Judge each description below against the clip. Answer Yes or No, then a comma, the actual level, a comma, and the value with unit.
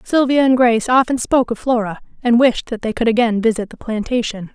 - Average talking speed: No, fast, 210 wpm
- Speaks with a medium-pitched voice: No, high, 235 Hz